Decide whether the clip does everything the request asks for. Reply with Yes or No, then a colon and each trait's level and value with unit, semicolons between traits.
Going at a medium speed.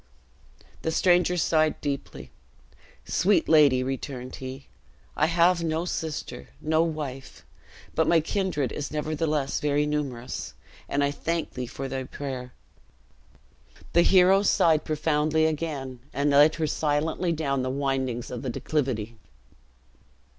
No: slow, 125 wpm